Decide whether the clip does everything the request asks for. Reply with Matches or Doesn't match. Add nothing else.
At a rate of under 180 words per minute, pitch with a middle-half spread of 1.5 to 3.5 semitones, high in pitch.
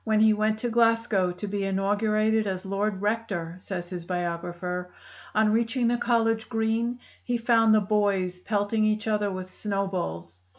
Matches